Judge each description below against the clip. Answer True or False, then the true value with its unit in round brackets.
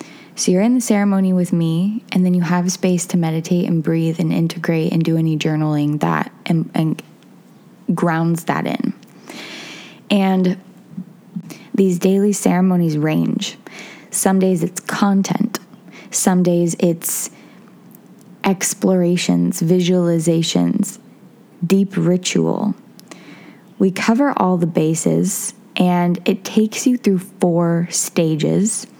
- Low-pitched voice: False (185 Hz)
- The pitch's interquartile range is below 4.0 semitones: True (2.8 semitones)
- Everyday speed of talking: False (115 wpm)